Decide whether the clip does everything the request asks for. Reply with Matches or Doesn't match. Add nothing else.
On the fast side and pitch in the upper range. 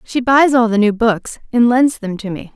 Matches